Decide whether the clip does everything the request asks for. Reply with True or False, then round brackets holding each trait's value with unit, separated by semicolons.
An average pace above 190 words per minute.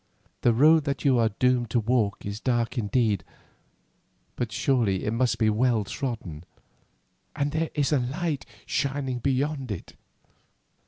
False (140 wpm)